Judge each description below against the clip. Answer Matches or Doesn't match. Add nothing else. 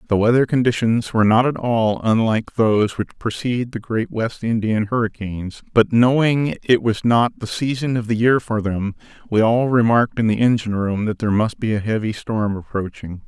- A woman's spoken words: Doesn't match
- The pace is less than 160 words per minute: Doesn't match